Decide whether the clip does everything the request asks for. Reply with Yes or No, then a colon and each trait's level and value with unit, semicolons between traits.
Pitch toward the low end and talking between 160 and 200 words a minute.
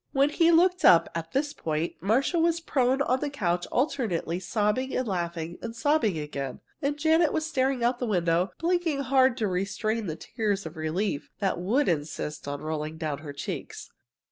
No: high, 215 Hz; average, 185 wpm